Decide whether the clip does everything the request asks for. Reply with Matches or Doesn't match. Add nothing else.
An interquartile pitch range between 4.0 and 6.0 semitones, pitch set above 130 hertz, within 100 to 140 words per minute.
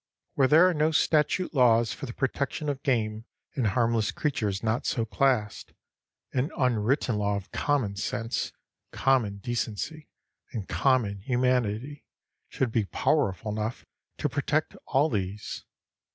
Doesn't match